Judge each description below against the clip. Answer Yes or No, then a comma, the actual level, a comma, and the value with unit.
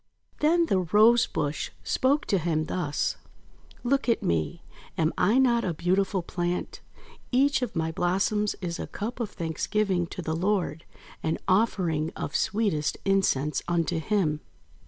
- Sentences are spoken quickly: No, average, 150 wpm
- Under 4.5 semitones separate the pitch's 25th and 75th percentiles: No, average, 4.9 semitones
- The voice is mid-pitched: Yes, medium, 180 Hz